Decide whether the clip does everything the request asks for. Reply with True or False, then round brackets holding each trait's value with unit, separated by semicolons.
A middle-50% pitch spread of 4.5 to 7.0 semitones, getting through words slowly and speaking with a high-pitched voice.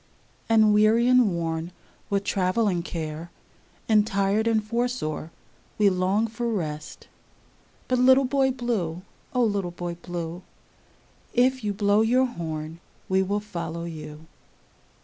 True (5.1 semitones; 130 wpm; 200 Hz)